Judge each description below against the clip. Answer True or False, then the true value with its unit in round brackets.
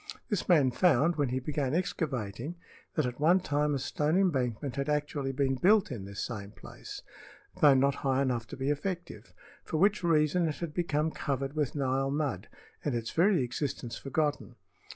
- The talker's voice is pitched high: False (145 Hz)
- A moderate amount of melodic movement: True (3.4 semitones)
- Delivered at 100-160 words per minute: False (175 wpm)